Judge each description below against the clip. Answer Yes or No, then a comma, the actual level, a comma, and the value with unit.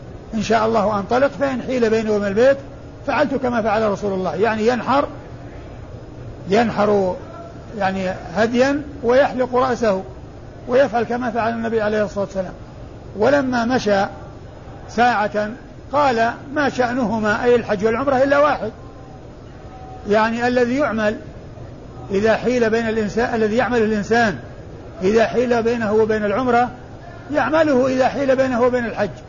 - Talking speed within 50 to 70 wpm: No, average, 125 wpm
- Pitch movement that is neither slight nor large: Yes, average, 3.1 semitones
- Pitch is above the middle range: Yes, high, 230 Hz